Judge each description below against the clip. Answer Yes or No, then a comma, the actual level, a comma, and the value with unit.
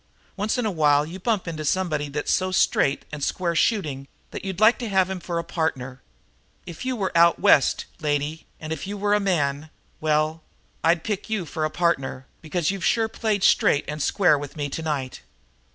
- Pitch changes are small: No, average, 4.5 semitones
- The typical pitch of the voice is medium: Yes, medium, 165 Hz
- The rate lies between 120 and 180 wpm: No, average, 200 wpm